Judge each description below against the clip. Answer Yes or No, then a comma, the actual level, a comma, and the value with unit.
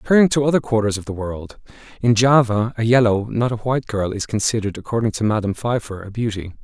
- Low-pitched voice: Yes, low, 110 Hz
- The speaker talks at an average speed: No, fast, 210 wpm